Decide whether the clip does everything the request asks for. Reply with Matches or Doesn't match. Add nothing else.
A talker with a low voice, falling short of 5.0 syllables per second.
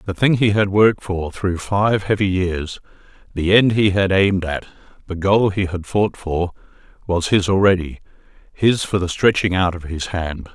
Matches